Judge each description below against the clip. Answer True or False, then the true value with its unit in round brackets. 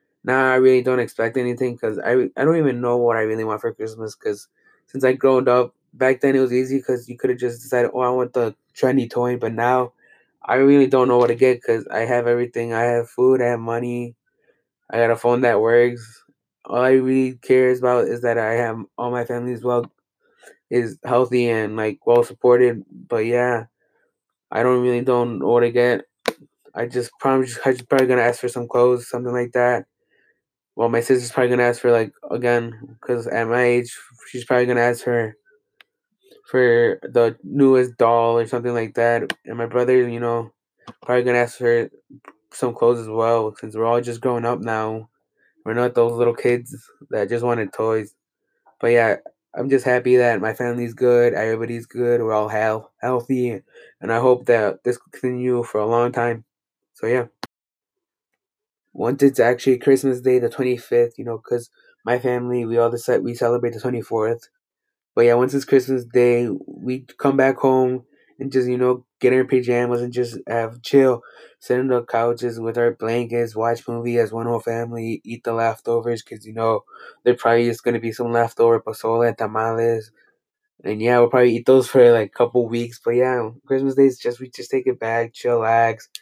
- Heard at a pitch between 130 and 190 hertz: False (120 Hz)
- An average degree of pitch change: False (1.4 semitones)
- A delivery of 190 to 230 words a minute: True (200 wpm)